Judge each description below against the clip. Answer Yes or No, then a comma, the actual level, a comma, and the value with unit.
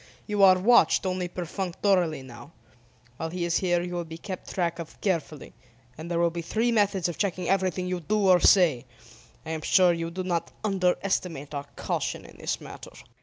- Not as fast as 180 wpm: No, average, 190 wpm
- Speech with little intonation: Yes, narrow, 2.2 semitones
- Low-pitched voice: No, medium, 175 Hz